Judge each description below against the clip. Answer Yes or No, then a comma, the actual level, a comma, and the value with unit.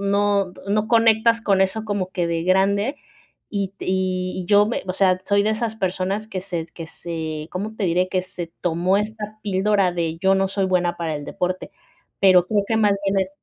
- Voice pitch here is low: No, high, 190 Hz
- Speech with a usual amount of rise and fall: No, narrow, 2.3 semitones